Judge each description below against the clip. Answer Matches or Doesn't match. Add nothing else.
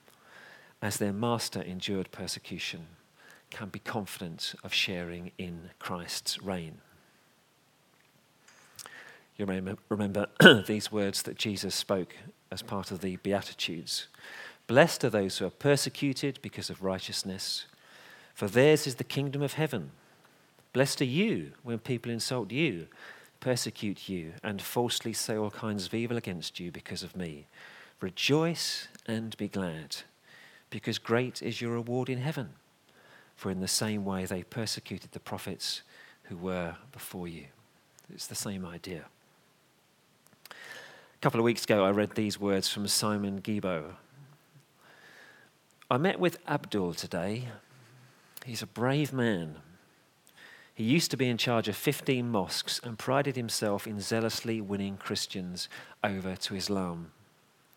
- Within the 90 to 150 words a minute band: Matches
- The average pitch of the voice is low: Matches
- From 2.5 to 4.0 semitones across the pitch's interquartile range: Doesn't match